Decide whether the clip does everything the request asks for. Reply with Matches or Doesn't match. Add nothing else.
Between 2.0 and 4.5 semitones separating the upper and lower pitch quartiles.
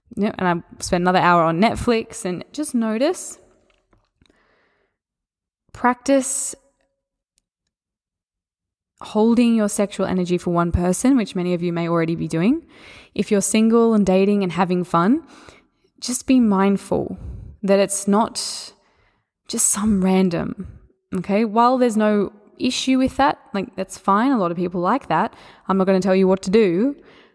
Doesn't match